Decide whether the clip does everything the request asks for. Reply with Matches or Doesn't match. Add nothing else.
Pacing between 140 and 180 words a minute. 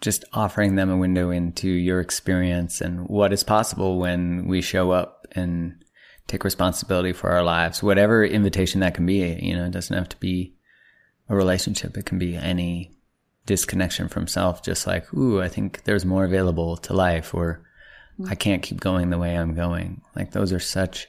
Doesn't match